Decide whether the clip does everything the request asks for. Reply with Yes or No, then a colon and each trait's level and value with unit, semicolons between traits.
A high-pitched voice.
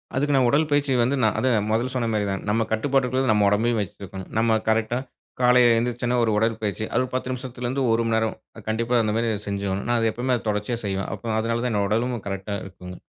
No: low, 115 Hz